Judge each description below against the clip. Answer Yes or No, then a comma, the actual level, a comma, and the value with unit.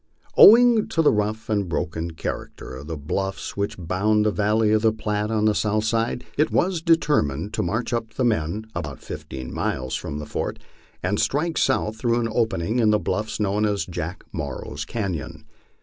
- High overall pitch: No, low, 105 Hz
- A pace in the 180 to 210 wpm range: Yes, average, 185 wpm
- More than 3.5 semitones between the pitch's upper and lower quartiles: Yes, average, 4.4 semitones